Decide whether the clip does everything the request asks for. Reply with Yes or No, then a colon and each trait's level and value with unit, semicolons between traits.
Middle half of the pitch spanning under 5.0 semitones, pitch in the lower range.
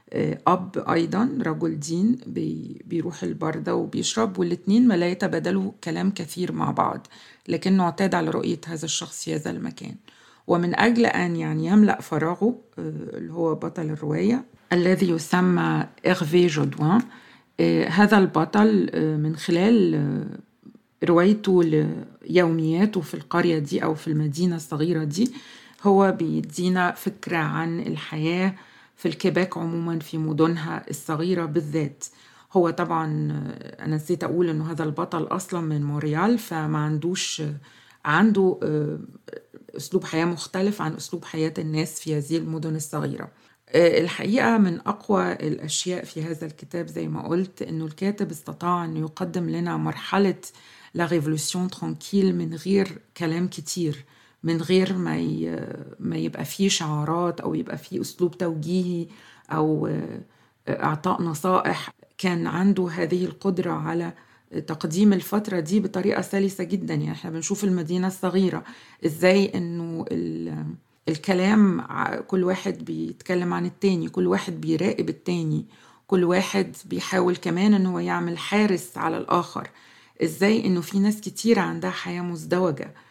No: average, 2.9 semitones; medium, 175 Hz